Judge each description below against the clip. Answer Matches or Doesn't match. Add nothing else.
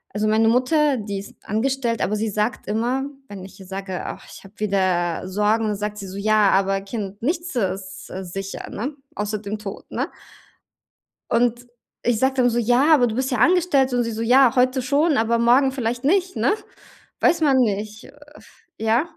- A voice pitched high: Matches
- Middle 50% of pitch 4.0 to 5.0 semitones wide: Matches